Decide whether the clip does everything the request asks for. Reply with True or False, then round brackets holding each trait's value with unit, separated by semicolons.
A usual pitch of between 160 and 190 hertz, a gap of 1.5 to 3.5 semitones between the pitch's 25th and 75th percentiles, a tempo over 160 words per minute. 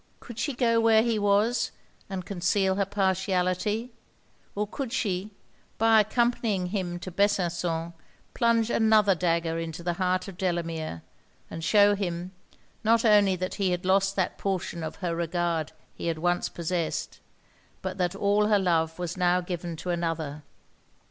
False (185 Hz; 3.1 semitones; 155 wpm)